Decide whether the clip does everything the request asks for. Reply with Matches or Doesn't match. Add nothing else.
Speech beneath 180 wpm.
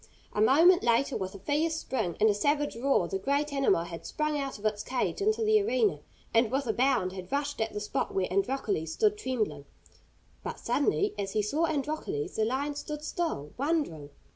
Doesn't match